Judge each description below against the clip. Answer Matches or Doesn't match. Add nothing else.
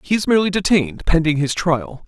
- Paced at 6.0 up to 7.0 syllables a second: Matches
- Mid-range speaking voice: Matches